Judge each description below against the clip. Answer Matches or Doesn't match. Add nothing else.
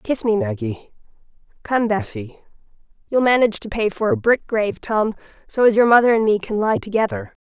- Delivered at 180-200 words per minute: Doesn't match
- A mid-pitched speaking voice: Doesn't match